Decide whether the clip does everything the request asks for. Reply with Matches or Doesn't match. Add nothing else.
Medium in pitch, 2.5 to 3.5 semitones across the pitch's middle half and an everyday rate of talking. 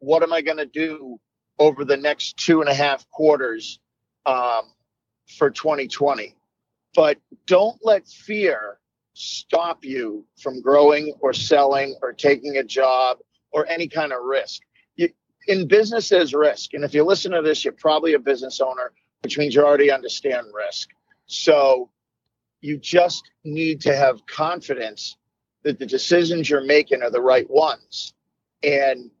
Matches